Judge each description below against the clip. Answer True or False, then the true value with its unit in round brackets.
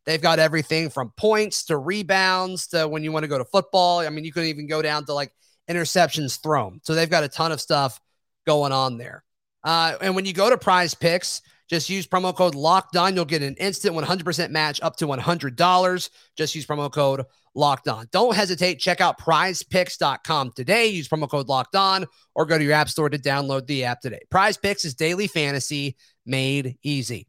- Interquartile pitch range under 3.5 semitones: False (4.0 semitones)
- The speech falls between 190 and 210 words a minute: True (205 wpm)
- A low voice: False (160 Hz)